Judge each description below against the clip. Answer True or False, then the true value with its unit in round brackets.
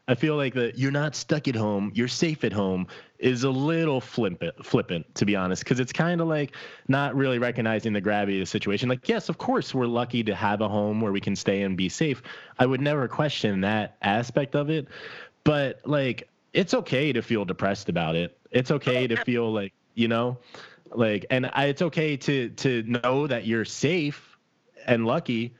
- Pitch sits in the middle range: False (125 Hz)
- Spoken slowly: False (205 wpm)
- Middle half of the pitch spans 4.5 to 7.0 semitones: True (4.8 semitones)